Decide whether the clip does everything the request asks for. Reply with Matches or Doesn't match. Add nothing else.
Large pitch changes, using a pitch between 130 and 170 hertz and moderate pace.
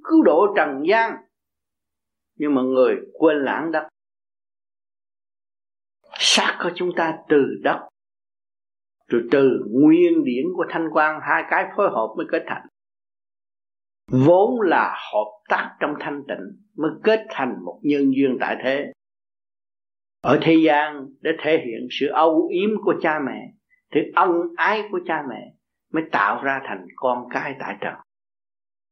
Doesn't match